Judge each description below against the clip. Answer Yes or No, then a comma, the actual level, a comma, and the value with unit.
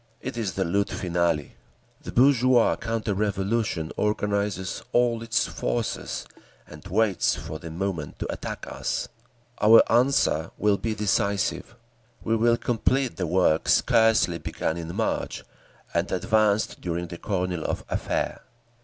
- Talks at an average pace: No, slow, 130 wpm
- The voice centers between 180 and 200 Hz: No, low, 100 Hz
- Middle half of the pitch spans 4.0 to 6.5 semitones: Yes, average, 4.5 semitones